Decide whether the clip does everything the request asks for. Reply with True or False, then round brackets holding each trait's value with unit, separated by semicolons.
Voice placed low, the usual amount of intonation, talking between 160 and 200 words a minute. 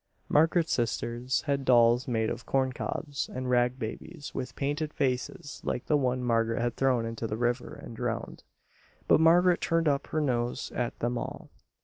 True (125 Hz; 3.3 semitones; 165 wpm)